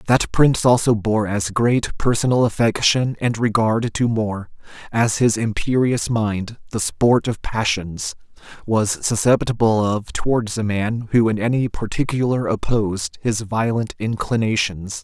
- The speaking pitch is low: Yes, low, 110 Hz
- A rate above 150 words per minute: No, slow, 135 wpm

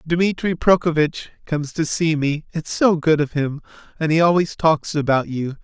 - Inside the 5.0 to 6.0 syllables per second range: No, 4.7 syllables/s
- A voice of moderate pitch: Yes, medium, 155 Hz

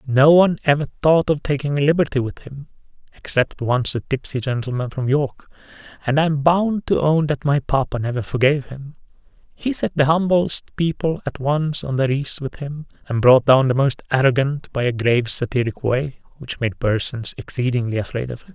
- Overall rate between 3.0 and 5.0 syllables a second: Yes, 3.9 syllables/s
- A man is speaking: Yes, male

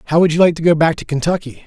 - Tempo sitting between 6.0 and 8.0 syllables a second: Yes, 7.6 syllables/s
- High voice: No, medium, 160 Hz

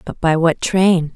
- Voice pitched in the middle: Yes, medium, 170 Hz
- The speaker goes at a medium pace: No, fast, 210 wpm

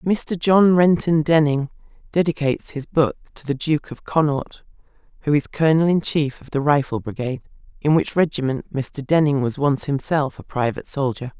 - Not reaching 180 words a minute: Yes, average, 170 wpm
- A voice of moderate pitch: Yes, medium, 150 Hz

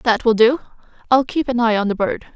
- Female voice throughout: Yes, female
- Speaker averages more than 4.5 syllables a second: Yes, 5.5 syllables/s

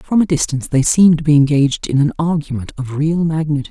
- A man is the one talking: No, female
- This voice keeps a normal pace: No, fast, 225 wpm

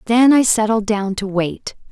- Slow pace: No, average, 190 wpm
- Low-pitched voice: No, high, 215 Hz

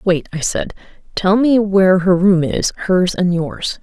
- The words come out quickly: No, average, 190 wpm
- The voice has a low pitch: No, medium, 185 Hz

